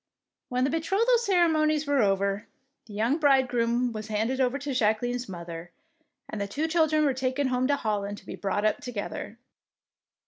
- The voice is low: No, very high, 250 Hz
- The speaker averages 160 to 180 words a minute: Yes, average, 175 wpm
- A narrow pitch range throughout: No, wide, 5.4 semitones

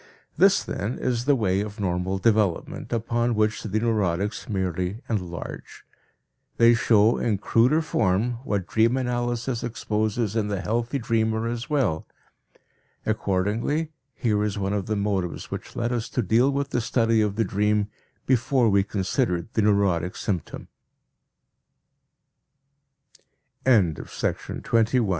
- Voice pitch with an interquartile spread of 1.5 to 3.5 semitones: Yes, average, 3.1 semitones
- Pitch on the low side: Yes, low, 110 Hz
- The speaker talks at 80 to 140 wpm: Yes, slow, 135 wpm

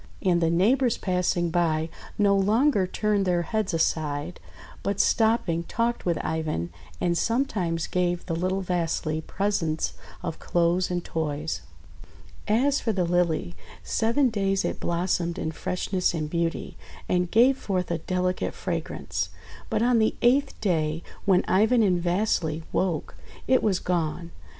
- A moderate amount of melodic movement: Yes, average, 3.8 semitones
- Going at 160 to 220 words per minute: No, average, 140 wpm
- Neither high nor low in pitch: Yes, medium, 180 Hz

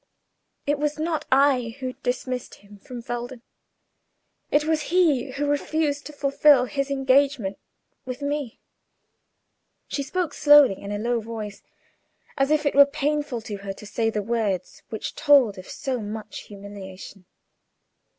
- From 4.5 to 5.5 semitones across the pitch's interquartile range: Yes, average, 5.0 semitones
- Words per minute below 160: Yes, average, 145 wpm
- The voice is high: Yes, very high, 260 Hz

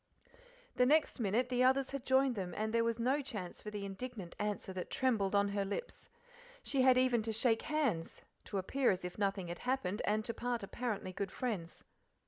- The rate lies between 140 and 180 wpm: No, average, 200 wpm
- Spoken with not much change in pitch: No, average, 4.4 semitones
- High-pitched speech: Yes, high, 225 Hz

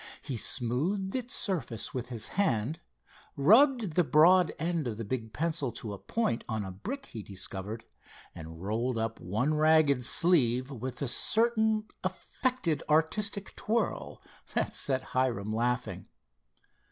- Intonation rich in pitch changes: Yes, wide, 8.3 semitones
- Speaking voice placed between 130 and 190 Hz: Yes, low, 135 Hz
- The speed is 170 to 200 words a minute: No, average, 140 wpm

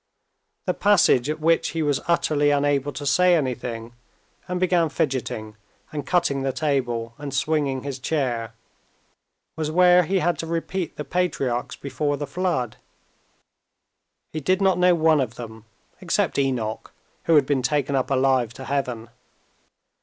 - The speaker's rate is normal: Yes, average, 150 wpm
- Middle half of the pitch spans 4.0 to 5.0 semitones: Yes, average, 4.3 semitones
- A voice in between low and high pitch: Yes, medium, 145 Hz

